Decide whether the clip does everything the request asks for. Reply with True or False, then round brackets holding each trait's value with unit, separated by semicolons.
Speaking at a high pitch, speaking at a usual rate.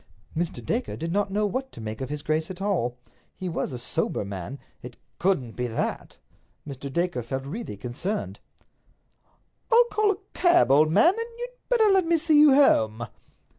False (175 Hz; 175 wpm)